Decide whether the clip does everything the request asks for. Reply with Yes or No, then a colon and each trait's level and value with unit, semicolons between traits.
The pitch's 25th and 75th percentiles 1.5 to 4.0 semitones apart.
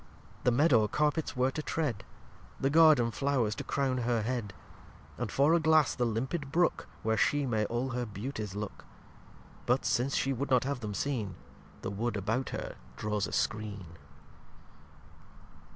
No: average, 4.6 semitones